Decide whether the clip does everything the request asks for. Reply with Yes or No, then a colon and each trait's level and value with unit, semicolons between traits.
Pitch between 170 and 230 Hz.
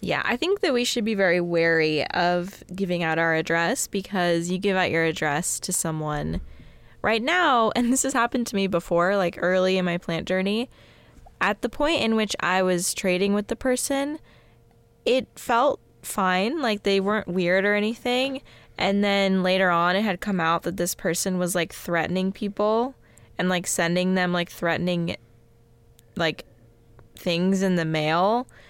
Yes: medium, 185 Hz